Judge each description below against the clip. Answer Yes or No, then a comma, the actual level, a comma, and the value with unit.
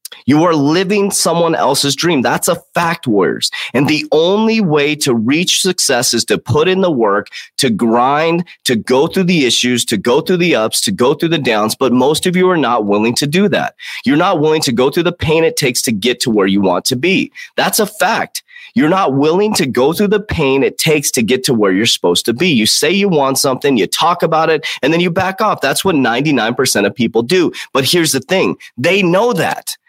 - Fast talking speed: Yes, fast, 235 wpm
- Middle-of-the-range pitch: Yes, medium, 160 Hz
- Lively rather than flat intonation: Yes, wide, 6.4 semitones